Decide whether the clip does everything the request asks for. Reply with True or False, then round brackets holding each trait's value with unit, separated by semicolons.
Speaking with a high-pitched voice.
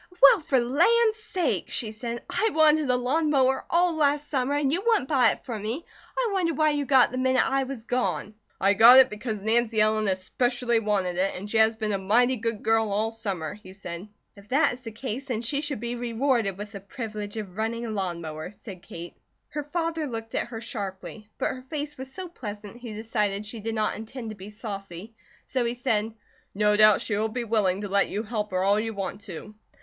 True (225 Hz)